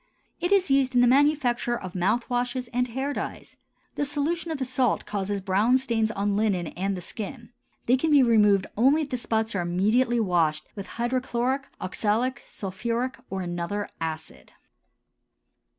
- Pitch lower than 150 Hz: No, high, 235 Hz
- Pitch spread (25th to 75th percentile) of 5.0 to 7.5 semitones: No, average, 4.6 semitones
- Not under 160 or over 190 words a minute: Yes, average, 165 wpm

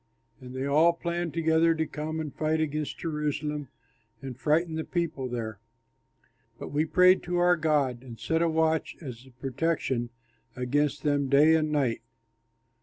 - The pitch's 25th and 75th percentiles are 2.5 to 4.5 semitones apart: Yes, average, 3.2 semitones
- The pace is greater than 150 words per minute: Yes, average, 160 wpm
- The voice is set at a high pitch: No, medium, 150 Hz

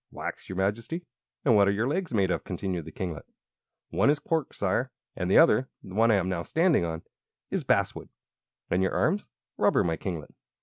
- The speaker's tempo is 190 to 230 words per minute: Yes, average, 200 wpm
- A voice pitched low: Yes, low, 100 Hz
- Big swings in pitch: Yes, wide, 6.3 semitones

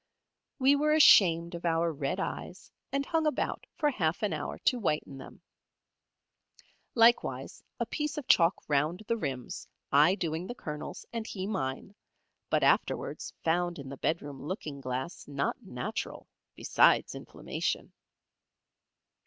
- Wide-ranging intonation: Yes, wide, 7.6 semitones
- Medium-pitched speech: Yes, medium, 175 Hz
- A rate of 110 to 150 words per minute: Yes, slow, 135 wpm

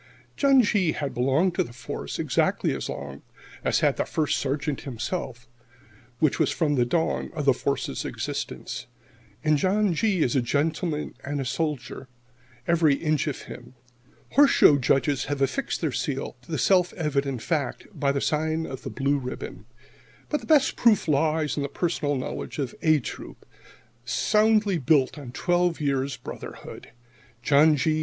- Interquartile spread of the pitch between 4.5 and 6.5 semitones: No, average, 3.7 semitones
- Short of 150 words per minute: No, average, 165 wpm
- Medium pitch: Yes, medium, 150 Hz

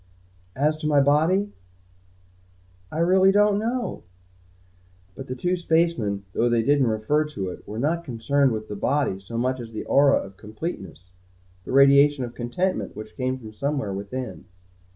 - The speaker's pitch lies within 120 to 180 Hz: Yes, low, 135 Hz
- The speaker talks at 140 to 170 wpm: Yes, average, 160 wpm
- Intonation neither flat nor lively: No, wide, 6.0 semitones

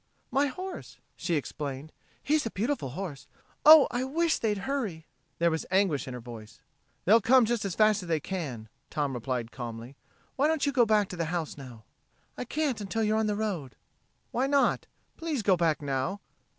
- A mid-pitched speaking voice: No, high, 195 Hz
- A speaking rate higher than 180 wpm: Yes, average, 190 wpm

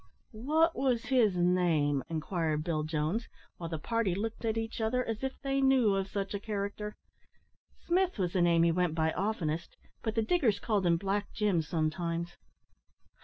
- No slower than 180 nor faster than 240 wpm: No, average, 170 wpm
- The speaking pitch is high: Yes, high, 195 Hz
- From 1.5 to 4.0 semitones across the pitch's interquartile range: No, average, 5.1 semitones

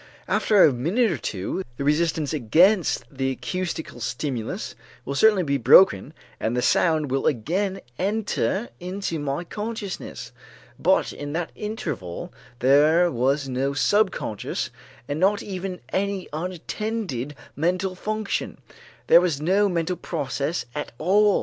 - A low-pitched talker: No, medium, 170 Hz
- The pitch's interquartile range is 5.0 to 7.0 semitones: Yes, wide, 5.6 semitones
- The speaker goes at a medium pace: No, slow, 130 wpm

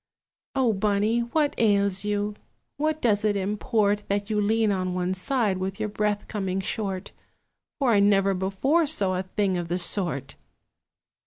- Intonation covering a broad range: No, narrow, 2.4 semitones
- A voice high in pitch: Yes, high, 205 Hz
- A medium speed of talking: Yes, average, 160 wpm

